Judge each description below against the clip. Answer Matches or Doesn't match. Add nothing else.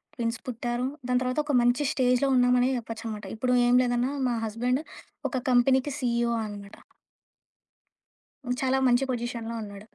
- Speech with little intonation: Matches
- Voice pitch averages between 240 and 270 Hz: Matches